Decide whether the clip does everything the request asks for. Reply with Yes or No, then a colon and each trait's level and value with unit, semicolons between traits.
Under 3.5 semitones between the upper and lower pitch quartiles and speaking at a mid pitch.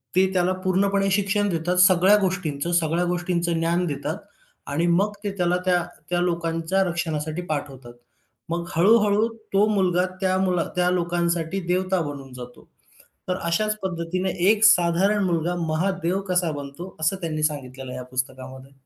Yes: average, 2.8 semitones; medium, 175 Hz